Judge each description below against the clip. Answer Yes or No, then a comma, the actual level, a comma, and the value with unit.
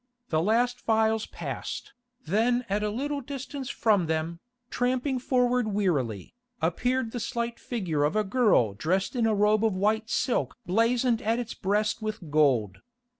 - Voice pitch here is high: Yes, high, 220 Hz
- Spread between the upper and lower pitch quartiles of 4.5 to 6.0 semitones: Yes, average, 4.8 semitones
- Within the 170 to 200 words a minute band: No, average, 155 wpm